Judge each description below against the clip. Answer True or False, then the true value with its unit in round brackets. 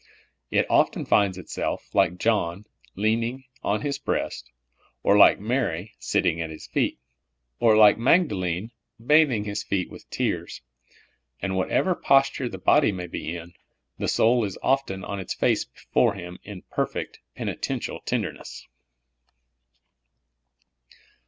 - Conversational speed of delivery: False (130 wpm)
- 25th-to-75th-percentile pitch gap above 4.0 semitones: True (4.7 semitones)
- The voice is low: True (105 Hz)